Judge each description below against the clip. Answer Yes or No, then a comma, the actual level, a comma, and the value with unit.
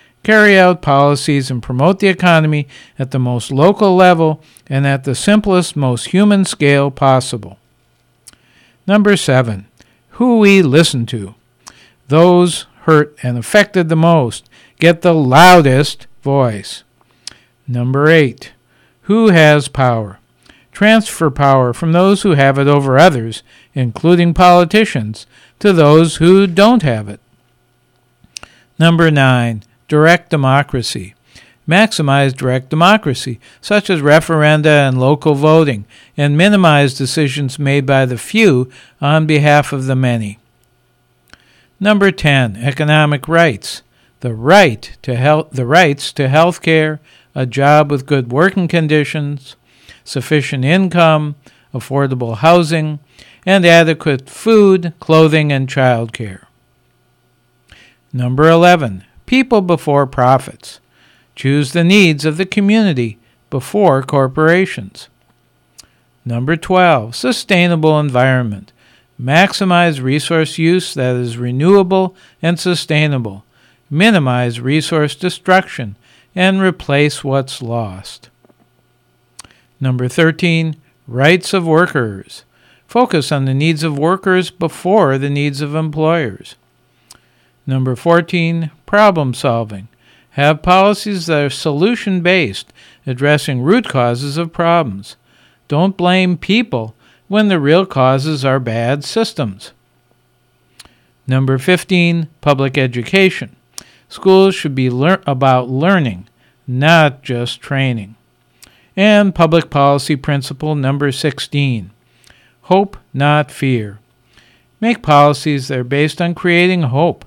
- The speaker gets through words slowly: Yes, slow, 110 wpm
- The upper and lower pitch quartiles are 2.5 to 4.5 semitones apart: No, average, 5.2 semitones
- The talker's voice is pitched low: No, medium, 145 Hz